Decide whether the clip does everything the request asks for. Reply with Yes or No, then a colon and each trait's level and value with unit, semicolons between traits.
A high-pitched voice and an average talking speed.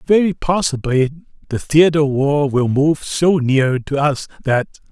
No: medium, 145 Hz; average, 160 wpm